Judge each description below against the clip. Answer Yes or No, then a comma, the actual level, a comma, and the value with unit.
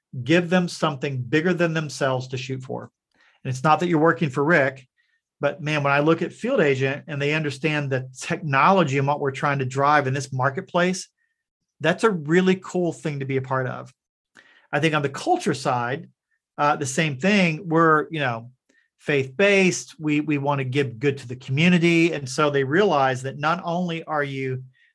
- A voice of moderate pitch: Yes, medium, 150 Hz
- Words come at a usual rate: Yes, average, 195 wpm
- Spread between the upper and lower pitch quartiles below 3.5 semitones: No, average, 3.8 semitones